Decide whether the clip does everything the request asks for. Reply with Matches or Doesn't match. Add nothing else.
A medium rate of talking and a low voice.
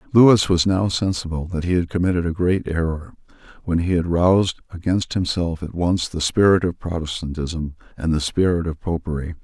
Matches